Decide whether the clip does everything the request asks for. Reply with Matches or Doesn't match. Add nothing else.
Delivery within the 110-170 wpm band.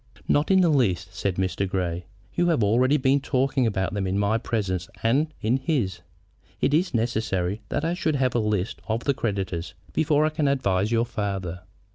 Doesn't match